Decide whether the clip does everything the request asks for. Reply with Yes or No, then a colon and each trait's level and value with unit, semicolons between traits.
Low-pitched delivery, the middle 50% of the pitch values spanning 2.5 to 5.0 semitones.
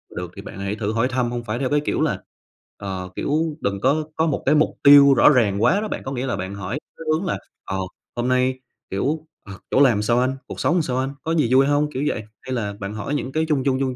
No: low, 130 Hz; wide, 5.4 semitones